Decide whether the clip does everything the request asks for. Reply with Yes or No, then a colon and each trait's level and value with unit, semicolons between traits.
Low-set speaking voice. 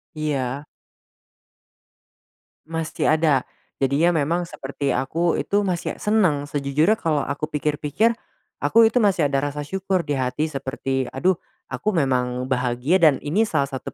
No: medium, 150 Hz